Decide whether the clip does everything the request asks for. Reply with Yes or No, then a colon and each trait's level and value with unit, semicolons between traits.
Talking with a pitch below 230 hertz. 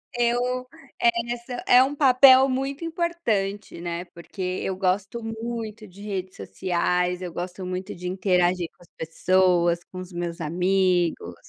Yes: high, 190 Hz